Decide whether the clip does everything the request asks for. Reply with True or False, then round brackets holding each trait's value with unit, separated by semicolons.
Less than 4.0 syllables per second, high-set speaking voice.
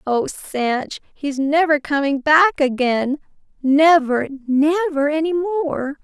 True (3.6 syllables/s; 290 Hz)